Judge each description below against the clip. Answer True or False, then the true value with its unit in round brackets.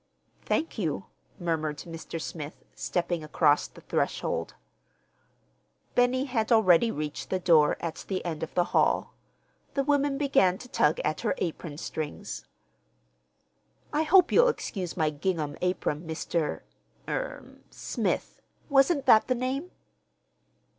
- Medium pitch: True (180 Hz)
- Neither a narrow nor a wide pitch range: False (8.6 semitones)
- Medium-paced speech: False (120 wpm)